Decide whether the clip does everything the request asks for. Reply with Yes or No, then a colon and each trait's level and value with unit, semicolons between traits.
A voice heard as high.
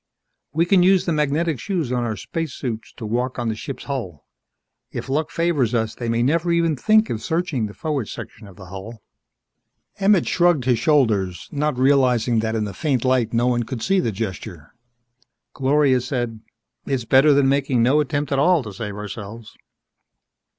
No: low, 130 Hz